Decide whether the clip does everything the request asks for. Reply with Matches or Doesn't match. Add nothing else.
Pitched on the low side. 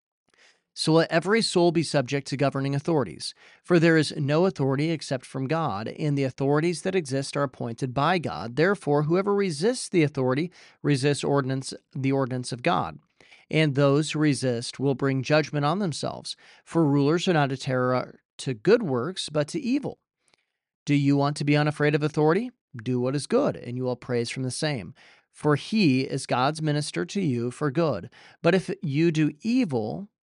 Doesn't match